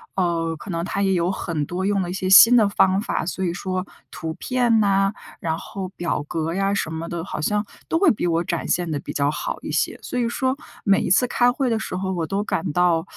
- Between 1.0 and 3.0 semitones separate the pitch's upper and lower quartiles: No, average, 3.4 semitones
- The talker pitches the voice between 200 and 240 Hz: No, medium, 185 Hz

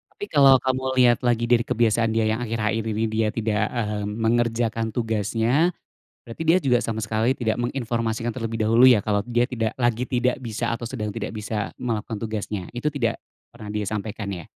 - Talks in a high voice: No, low, 115 Hz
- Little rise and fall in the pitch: Yes, narrow, 1.9 semitones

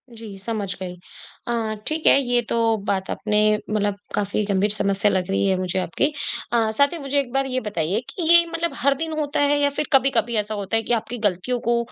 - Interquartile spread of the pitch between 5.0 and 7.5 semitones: Yes, wide, 5.4 semitones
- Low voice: No, high, 225 Hz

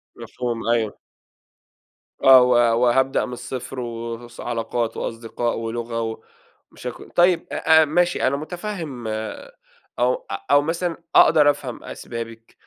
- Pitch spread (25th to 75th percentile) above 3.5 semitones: Yes, average, 4.0 semitones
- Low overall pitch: Yes, low, 125 Hz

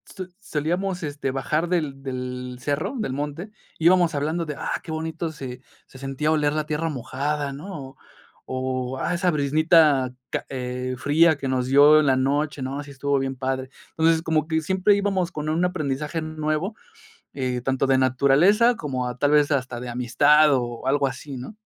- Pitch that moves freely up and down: No, average, 3.4 semitones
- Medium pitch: Yes, medium, 145 Hz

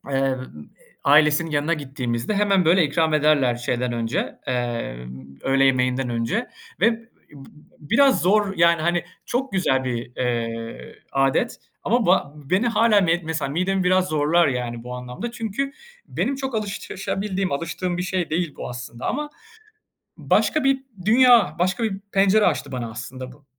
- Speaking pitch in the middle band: Yes, medium, 160 Hz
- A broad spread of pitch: Yes, wide, 7.5 semitones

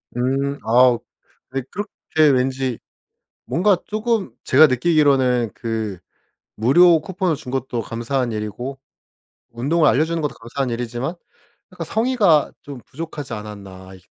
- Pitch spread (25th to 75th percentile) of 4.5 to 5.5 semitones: Yes, average, 5.1 semitones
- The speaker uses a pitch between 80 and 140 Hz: Yes, low, 135 Hz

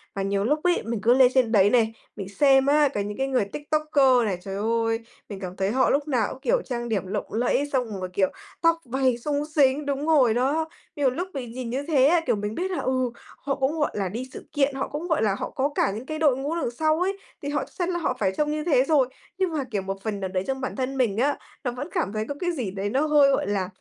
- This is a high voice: Yes, very high, 260 Hz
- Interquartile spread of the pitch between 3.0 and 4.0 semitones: No, average, 5.2 semitones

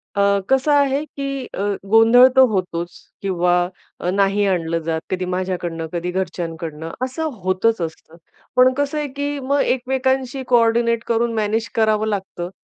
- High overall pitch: Yes, high, 220 Hz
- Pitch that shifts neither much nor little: No, wide, 6.4 semitones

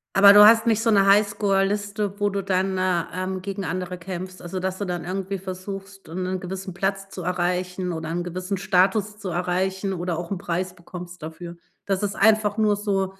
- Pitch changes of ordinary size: No, narrow, 1.7 semitones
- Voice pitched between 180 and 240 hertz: Yes, high, 190 Hz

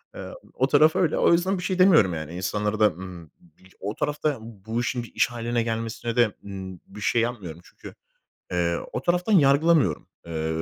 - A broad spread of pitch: Yes, wide, 7.9 semitones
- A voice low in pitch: Yes, low, 115 Hz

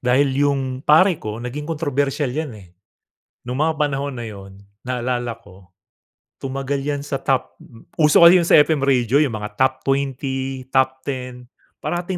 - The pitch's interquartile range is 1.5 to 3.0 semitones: Yes, narrow, 2.6 semitones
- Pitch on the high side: No, low, 135 Hz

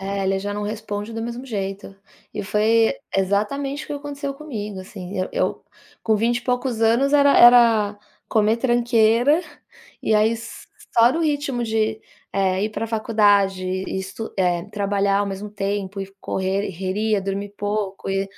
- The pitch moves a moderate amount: Yes, average, 3.1 semitones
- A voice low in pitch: No, high, 210 Hz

